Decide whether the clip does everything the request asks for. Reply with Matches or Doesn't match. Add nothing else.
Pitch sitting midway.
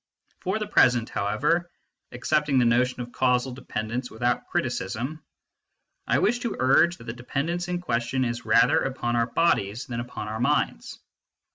Doesn't match